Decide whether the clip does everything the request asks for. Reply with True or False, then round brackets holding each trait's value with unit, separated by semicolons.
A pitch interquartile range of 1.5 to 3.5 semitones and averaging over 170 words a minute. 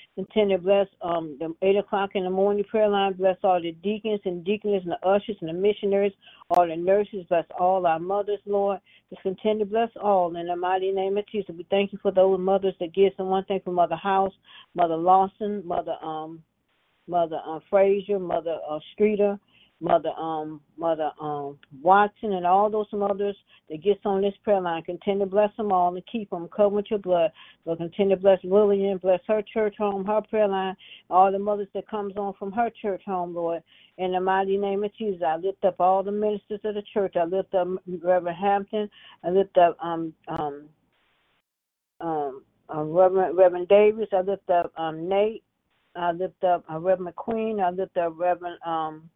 True (2.6 semitones; 200 wpm)